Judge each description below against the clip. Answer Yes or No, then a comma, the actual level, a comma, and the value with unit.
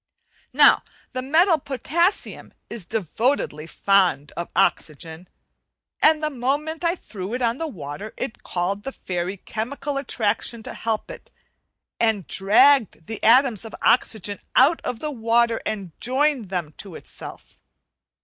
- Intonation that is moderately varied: No, wide, 6.0 semitones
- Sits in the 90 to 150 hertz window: No, high, 230 Hz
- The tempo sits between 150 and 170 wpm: No, average, 140 wpm